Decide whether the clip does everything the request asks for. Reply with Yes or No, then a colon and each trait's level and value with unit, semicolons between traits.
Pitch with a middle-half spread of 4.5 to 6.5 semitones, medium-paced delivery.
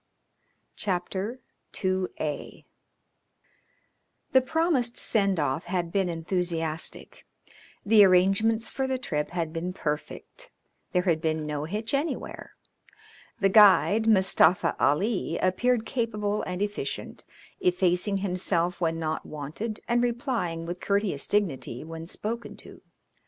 No: average, 5.1 semitones; slow, 115 wpm